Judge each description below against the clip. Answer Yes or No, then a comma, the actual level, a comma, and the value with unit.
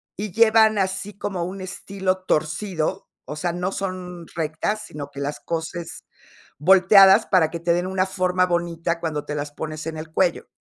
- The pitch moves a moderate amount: Yes, average, 3.0 semitones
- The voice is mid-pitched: Yes, medium, 175 Hz